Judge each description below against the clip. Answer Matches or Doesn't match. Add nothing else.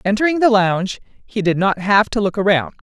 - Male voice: Doesn't match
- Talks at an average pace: Doesn't match